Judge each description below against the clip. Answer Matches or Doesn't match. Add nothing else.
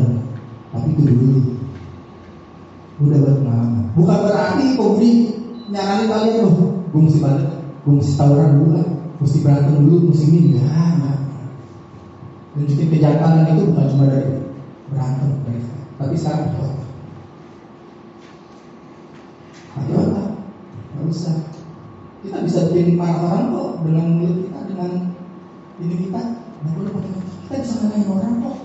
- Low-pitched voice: Doesn't match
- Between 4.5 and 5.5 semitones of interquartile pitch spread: Matches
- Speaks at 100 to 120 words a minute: Doesn't match